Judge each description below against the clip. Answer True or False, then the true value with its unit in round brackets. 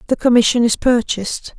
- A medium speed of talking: True (150 wpm)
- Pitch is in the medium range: False (235 Hz)